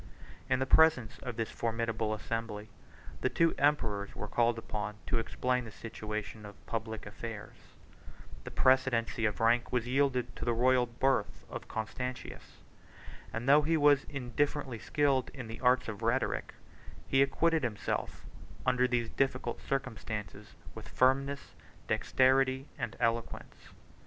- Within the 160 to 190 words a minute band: No, slow, 135 wpm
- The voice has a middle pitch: No, low, 120 Hz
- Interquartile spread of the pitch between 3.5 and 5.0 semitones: No, average, 3.0 semitones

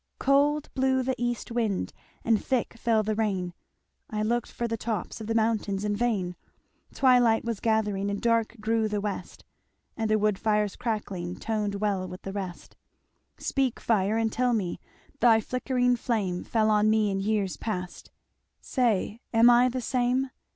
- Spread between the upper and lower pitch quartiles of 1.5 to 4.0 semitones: Yes, average, 2.8 semitones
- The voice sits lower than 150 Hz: No, high, 220 Hz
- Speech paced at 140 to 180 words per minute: Yes, average, 165 wpm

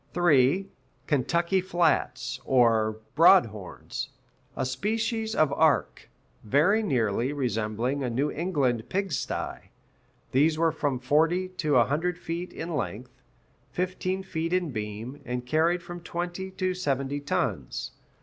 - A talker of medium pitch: Yes, medium, 150 Hz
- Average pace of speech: No, slow, 130 wpm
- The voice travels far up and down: Yes, wide, 5.8 semitones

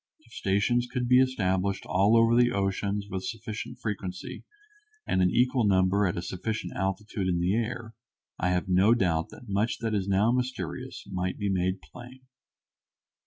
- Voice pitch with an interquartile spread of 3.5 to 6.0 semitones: Yes, average, 4.0 semitones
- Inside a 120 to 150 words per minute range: No, average, 165 wpm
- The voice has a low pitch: Yes, low, 100 Hz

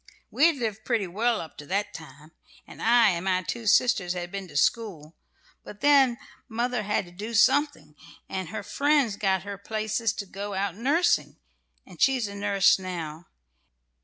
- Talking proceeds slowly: No, average, 175 wpm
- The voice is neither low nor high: No, high, 205 Hz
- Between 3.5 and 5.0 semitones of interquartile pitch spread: Yes, average, 4.3 semitones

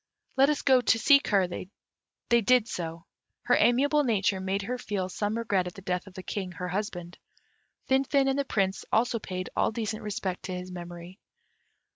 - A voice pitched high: Yes, high, 200 Hz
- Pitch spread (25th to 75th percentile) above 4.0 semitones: Yes, average, 4.9 semitones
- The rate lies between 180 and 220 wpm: Yes, average, 185 wpm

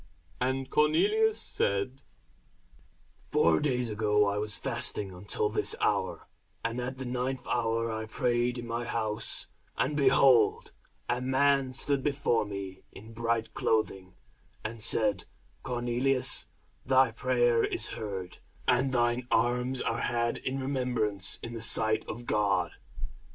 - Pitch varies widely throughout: No, average, 3.1 semitones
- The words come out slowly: Yes, slow, 130 wpm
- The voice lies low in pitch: Yes, low, 120 Hz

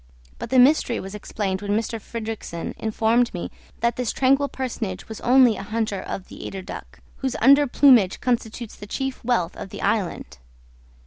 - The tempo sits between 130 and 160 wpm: No, average, 175 wpm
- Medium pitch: No, high, 225 Hz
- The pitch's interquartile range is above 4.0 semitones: No, average, 3.6 semitones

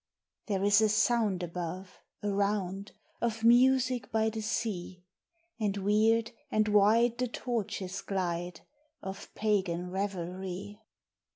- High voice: Yes, high, 205 Hz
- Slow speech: Yes, slow, 110 wpm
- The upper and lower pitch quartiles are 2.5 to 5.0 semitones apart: Yes, average, 2.9 semitones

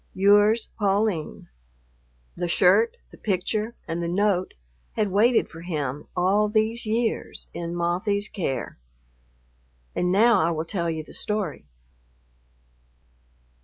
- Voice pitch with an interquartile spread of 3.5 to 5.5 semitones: Yes, average, 3.9 semitones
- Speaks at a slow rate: Yes, slow, 120 wpm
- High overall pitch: Yes, high, 195 Hz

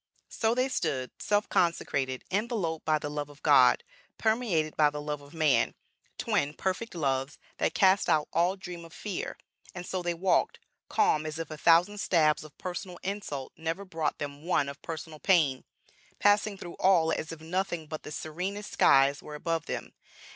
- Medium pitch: Yes, medium, 165 Hz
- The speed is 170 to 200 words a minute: Yes, average, 175 wpm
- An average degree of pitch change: Yes, average, 4.0 semitones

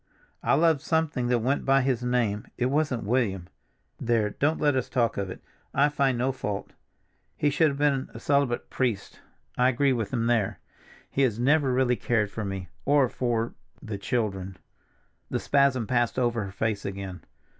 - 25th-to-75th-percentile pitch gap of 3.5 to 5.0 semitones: Yes, average, 4.2 semitones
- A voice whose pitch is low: Yes, low, 125 Hz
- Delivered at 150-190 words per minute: Yes, average, 175 wpm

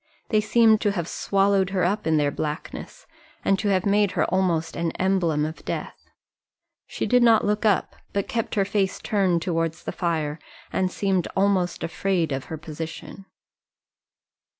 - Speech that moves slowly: No, average, 165 wpm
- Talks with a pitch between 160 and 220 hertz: Yes, high, 190 Hz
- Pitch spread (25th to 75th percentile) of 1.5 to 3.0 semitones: No, average, 3.5 semitones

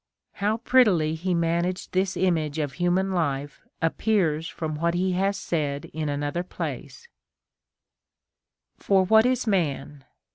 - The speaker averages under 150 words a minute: Yes, average, 140 wpm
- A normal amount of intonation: Yes, average, 3.8 semitones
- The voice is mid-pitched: Yes, medium, 175 Hz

